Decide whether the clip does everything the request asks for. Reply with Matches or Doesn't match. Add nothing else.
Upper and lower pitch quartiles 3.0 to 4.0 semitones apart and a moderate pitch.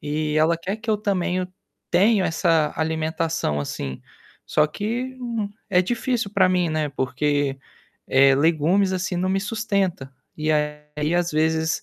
Doesn't match